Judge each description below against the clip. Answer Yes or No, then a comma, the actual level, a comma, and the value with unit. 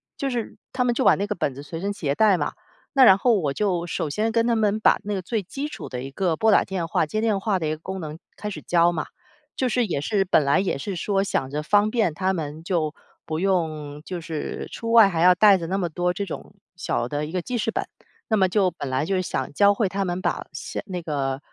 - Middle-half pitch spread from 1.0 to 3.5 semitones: No, average, 4.8 semitones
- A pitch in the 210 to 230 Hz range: No, medium, 185 Hz